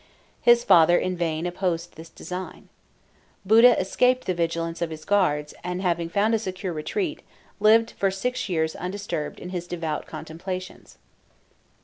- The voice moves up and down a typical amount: Yes, average, 3.3 semitones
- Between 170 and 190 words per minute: No, average, 145 wpm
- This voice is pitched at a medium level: Yes, medium, 180 Hz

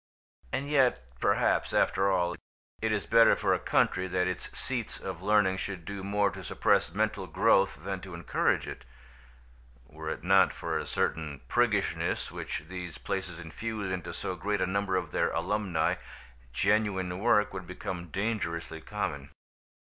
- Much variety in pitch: No, average, 3.0 semitones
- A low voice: Yes, very low, 95 Hz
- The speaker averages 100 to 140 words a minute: No, average, 155 wpm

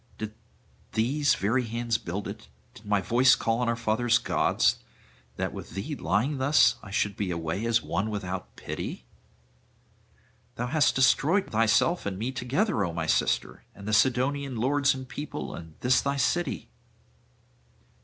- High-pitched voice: No, low, 115 Hz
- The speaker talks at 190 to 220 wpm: No, average, 155 wpm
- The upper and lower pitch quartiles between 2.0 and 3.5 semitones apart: No, average, 4.4 semitones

